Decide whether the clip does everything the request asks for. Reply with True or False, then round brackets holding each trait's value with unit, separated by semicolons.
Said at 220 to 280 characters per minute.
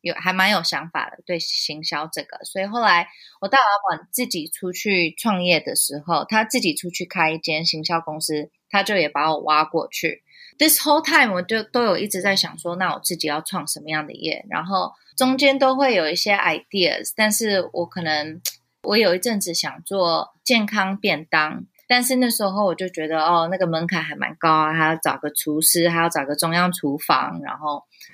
False (310 characters per minute)